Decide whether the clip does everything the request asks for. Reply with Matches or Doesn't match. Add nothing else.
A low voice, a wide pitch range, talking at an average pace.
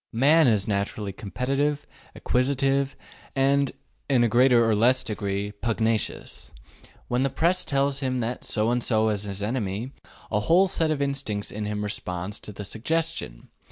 Doesn't match